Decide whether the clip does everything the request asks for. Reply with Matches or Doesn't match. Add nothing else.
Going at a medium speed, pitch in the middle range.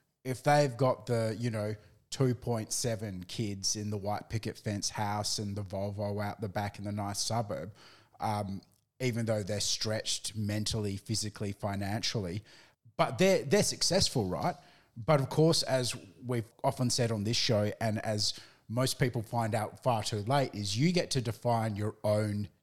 Doesn't match